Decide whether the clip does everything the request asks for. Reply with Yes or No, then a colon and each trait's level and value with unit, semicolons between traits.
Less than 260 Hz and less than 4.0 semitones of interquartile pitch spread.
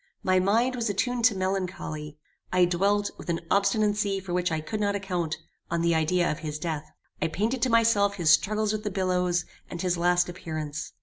Yes: medium, 185 Hz; average, 3.3 semitones